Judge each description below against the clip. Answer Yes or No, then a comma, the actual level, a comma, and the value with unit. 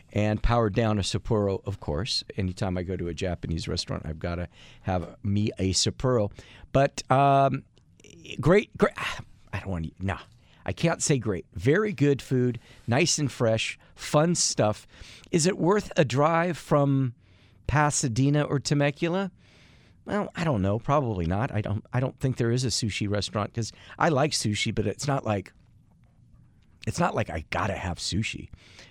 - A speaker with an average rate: Yes, average, 175 wpm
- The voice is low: Yes, low, 110 Hz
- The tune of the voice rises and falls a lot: Yes, wide, 6.2 semitones